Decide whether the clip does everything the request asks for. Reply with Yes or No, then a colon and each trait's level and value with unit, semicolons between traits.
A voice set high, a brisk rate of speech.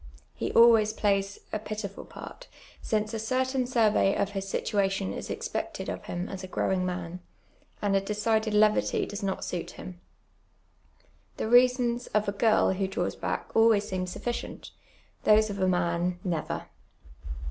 No: high, 205 Hz; average, 155 wpm